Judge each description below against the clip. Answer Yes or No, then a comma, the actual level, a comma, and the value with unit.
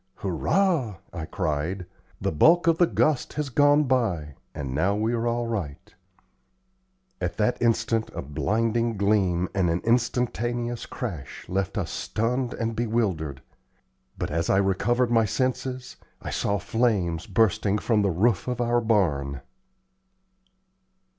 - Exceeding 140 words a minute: No, slow, 135 wpm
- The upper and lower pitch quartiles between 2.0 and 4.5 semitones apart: No, average, 4.9 semitones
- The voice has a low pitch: Yes, low, 110 Hz